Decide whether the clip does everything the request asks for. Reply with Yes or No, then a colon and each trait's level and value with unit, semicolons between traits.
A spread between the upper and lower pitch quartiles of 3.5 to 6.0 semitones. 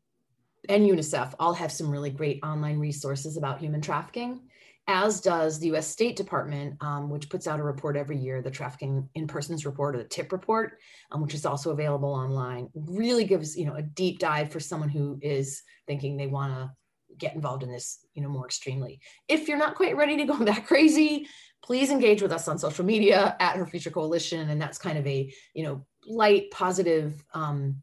Yes: average, 4.9 semitones